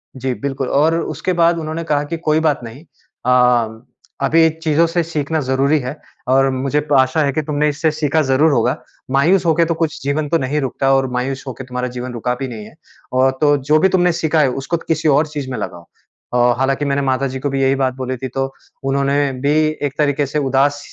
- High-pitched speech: No, medium, 140 Hz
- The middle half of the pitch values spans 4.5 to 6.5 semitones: No, average, 2.9 semitones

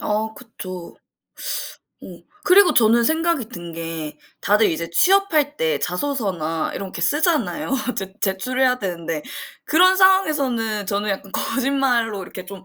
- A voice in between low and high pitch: No, high, 215 Hz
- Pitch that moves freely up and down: Yes, wide, 7.5 semitones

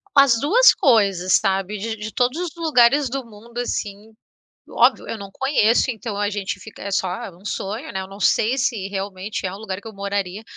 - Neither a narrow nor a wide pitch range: Yes, average, 3.7 semitones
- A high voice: Yes, high, 210 Hz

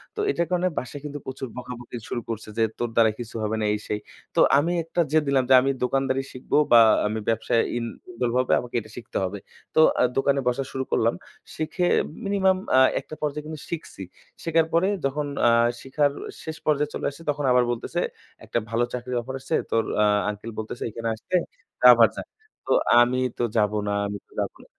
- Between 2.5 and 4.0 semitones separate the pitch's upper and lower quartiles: No, average, 4.5 semitones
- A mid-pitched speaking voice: No, low, 130 Hz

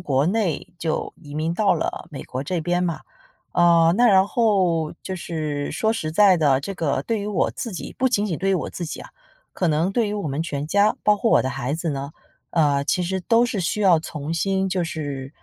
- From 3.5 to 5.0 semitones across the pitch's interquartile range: Yes, average, 4.5 semitones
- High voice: No, medium, 170 Hz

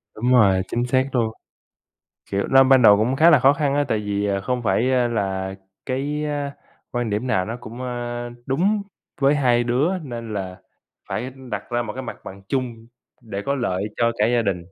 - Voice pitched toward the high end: No, low, 120 Hz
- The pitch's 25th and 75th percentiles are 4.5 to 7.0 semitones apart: No, average, 3.8 semitones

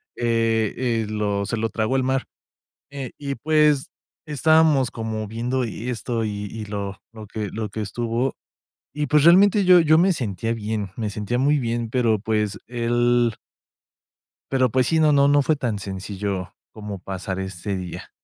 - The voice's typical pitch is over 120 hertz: No, low, 115 Hz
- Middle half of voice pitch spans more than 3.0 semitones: Yes, average, 4.2 semitones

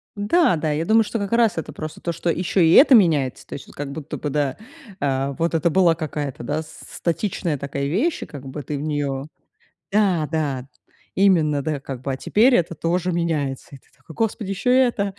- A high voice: No, medium, 160 Hz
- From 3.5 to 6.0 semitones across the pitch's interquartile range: Yes, average, 5.1 semitones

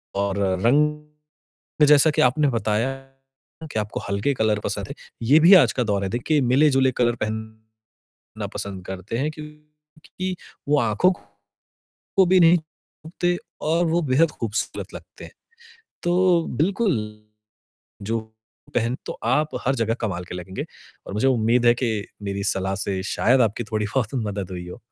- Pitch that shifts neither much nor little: No, wide, 6.3 semitones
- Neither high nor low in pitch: No, low, 120 Hz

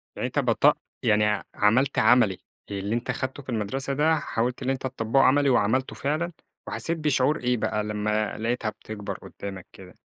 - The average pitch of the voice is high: No, low, 120 Hz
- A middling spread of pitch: Yes, average, 4.2 semitones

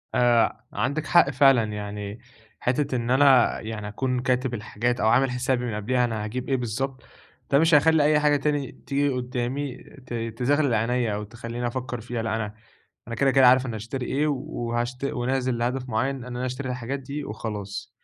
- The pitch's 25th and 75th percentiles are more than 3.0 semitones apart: No, narrow, 2.6 semitones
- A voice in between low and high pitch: No, low, 125 Hz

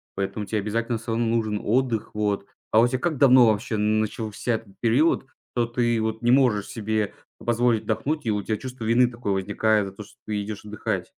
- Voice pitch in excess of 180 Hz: No, low, 110 Hz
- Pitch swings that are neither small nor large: No, narrow, 2.2 semitones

